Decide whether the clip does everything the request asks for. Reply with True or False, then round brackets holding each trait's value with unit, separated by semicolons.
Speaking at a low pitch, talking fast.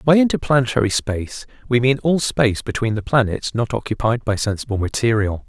False (120 Hz; 165 wpm)